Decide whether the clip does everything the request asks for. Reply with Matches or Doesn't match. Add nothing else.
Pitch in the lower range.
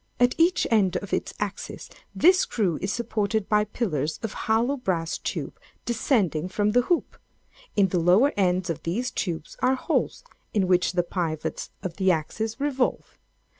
Doesn't match